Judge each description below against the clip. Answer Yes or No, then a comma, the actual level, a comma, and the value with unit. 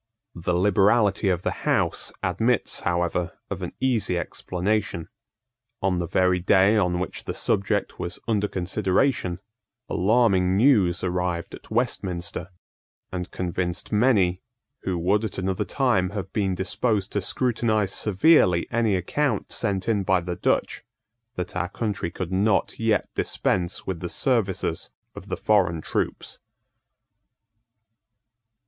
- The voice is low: Yes, very low, 95 Hz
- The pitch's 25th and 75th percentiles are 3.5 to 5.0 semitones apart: No, average, 3.1 semitones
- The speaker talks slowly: Yes, slow, 130 wpm